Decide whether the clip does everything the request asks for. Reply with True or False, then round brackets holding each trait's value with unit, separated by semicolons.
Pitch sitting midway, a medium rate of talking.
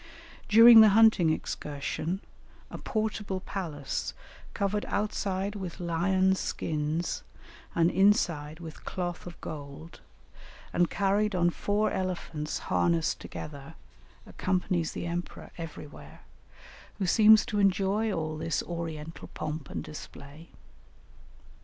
False (175 Hz; 110 wpm)